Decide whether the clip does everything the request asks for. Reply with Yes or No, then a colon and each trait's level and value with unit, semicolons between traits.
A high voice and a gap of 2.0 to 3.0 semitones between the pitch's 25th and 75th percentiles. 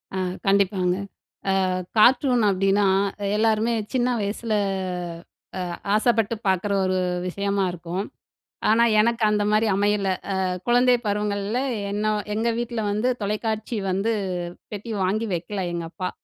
Yes: high, 210 Hz; narrow, 2.5 semitones